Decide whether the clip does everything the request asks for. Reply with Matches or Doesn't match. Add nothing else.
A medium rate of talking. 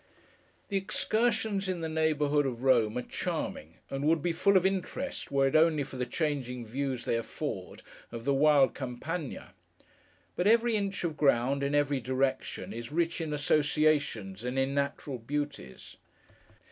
Matches